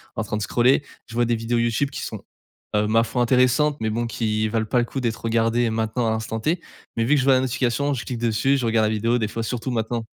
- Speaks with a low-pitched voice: Yes, low, 115 Hz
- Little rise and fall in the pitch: Yes, narrow, 2.0 semitones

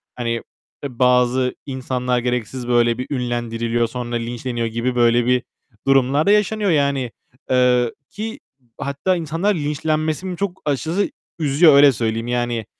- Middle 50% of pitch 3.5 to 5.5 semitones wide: Yes, average, 3.9 semitones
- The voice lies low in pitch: Yes, low, 125 Hz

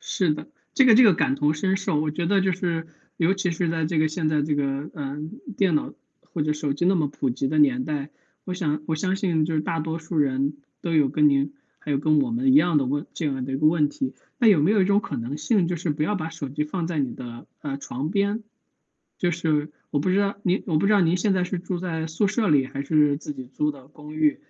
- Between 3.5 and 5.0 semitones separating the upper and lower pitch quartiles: Yes, average, 3.9 semitones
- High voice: No, medium, 155 Hz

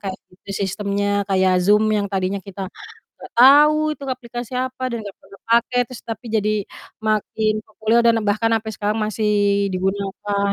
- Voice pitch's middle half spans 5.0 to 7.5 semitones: No, average, 2.7 semitones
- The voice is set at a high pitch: Yes, high, 215 Hz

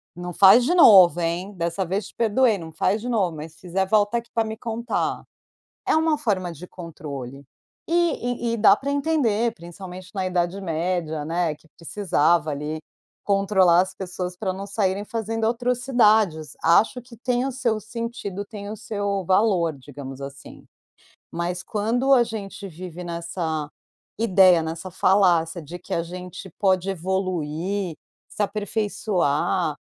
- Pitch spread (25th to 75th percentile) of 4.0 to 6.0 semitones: Yes, average, 4.3 semitones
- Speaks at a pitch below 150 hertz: No, high, 190 Hz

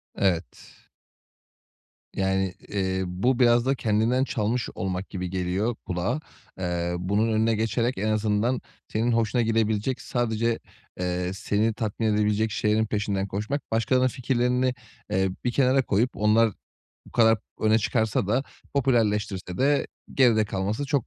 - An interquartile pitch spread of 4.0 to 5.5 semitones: No, average, 3.6 semitones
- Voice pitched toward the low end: Yes, low, 110 Hz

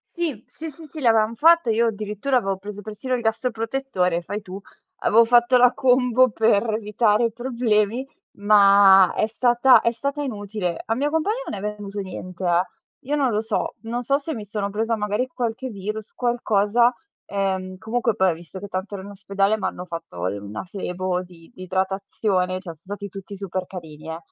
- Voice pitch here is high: Yes, high, 210 Hz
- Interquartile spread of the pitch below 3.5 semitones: No, average, 4.0 semitones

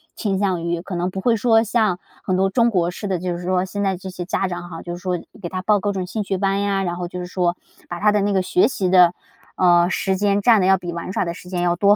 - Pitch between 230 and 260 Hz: No, medium, 185 Hz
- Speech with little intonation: Yes, narrow, 2.2 semitones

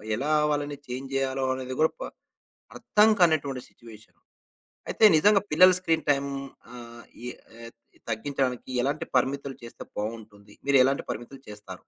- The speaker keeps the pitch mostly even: No, average, 3.6 semitones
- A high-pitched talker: No, low, 135 Hz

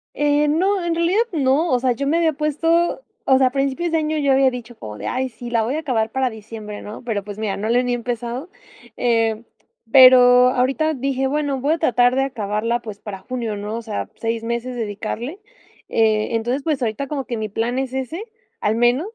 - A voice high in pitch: Yes, very high, 250 Hz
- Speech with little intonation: No, average, 3.9 semitones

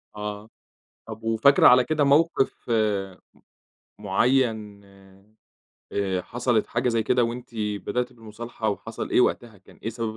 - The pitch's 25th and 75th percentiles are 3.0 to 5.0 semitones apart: No, narrow, 2.6 semitones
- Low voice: Yes, low, 115 Hz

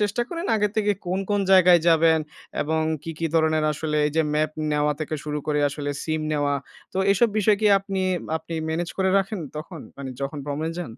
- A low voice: No, medium, 160 Hz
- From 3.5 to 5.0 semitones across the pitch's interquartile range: Yes, average, 4.1 semitones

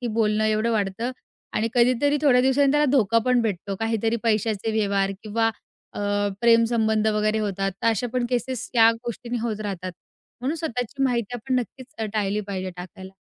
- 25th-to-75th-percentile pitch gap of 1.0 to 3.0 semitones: Yes, narrow, 2.6 semitones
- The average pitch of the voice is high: Yes, high, 225 Hz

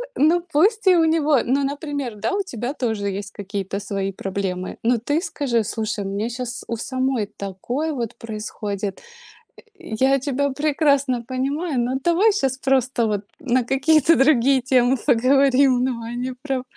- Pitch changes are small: No, average, 4.0 semitones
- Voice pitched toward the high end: Yes, very high, 255 Hz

